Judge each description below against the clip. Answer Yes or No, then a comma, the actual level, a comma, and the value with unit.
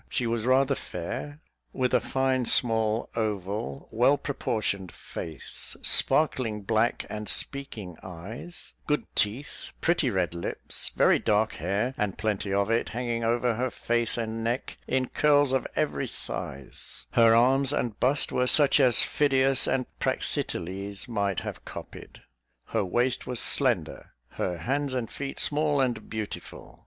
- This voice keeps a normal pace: Yes, average, 145 wpm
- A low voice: Yes, low, 120 Hz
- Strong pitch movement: No, average, 4.1 semitones